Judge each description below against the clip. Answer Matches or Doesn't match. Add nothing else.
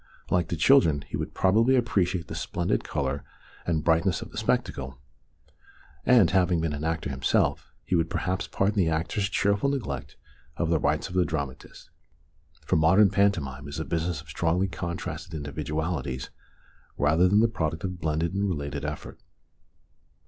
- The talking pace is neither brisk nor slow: Matches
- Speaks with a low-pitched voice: Matches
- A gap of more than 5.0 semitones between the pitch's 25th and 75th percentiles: Doesn't match